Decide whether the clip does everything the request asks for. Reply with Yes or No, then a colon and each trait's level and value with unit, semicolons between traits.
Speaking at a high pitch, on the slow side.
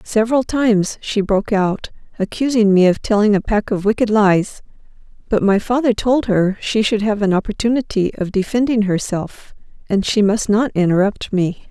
No: high, 210 Hz; average, 170 wpm